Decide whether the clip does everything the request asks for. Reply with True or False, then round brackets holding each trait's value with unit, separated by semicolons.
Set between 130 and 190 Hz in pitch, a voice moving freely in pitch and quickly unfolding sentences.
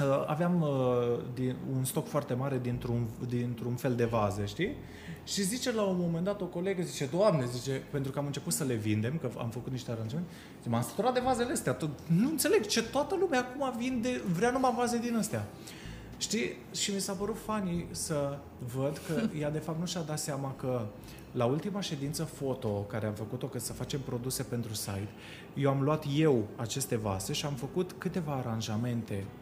True (140 Hz; 6.9 semitones; 195 wpm)